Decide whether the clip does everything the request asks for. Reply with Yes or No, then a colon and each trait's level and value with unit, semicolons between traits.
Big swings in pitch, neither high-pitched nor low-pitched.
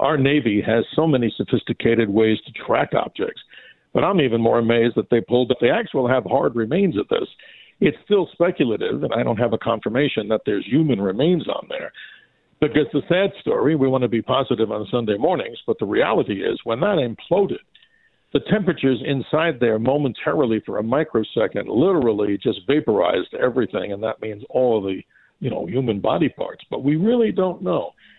No: wide, 5.7 semitones; low, 130 Hz